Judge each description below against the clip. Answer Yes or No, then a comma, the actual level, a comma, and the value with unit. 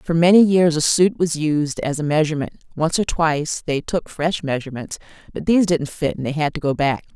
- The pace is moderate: No, fast, 225 wpm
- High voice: No, medium, 160 Hz